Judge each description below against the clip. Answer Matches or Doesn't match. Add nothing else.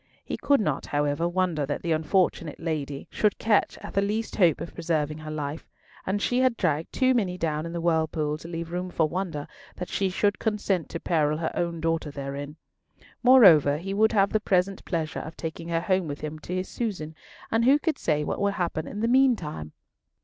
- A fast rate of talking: Matches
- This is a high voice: Doesn't match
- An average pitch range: Matches